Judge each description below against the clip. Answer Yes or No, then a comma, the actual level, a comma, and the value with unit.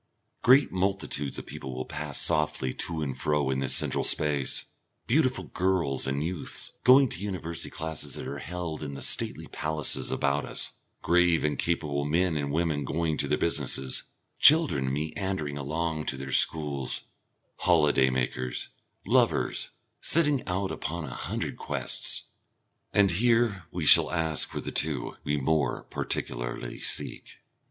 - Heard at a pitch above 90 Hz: No, very low, 75 Hz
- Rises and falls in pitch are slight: No, average, 4.0 semitones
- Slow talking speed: No, average, 150 wpm